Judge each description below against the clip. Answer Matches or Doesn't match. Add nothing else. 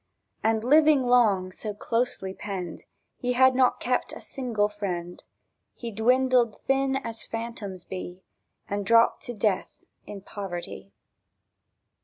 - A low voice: Doesn't match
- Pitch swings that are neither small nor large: Matches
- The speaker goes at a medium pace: Doesn't match